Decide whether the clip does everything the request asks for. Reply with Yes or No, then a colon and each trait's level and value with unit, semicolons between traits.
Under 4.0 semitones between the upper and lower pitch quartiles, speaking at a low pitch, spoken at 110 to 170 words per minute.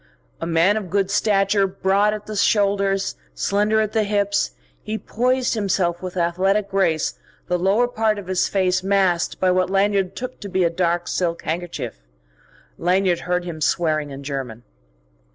No: average, 2.8 semitones; high, 190 Hz; average, 165 wpm